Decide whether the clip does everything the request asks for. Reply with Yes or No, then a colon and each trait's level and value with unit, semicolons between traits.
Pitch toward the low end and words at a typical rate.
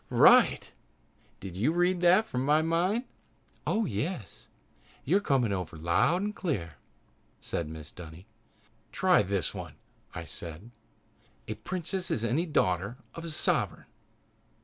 No: low, 130 Hz; slow, 125 wpm